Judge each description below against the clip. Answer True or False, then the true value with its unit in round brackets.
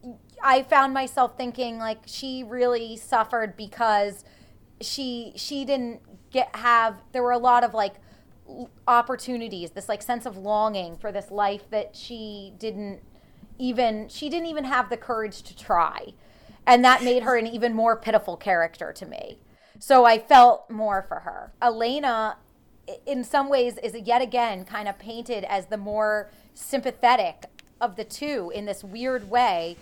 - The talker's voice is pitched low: False (235 Hz)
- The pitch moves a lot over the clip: False (2.9 semitones)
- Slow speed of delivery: False (160 wpm)